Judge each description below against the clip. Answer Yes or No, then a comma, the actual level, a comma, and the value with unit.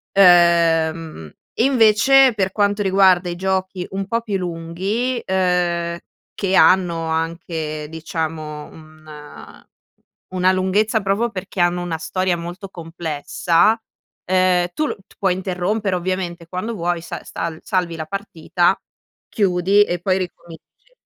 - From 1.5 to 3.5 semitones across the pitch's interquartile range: Yes, average, 2.7 semitones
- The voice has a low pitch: No, medium, 180 Hz